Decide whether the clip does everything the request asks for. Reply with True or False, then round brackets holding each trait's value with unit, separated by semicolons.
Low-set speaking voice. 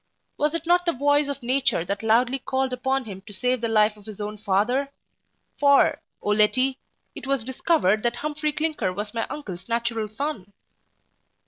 False (245 Hz)